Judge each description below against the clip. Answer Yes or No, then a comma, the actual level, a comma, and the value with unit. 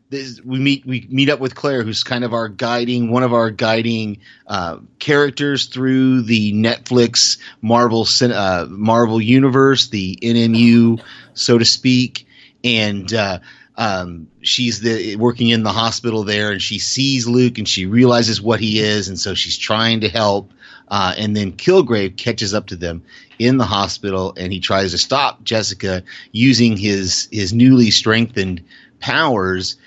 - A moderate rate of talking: Yes, average, 160 wpm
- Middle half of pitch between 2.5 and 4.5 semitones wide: Yes, average, 3.2 semitones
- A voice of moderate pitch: No, low, 115 Hz